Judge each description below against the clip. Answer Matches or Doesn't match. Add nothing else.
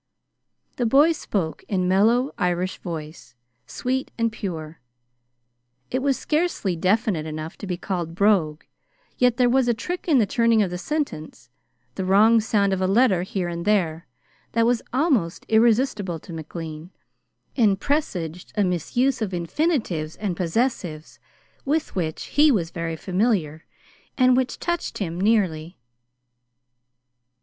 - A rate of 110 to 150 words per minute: Matches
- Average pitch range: Doesn't match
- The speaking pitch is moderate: Doesn't match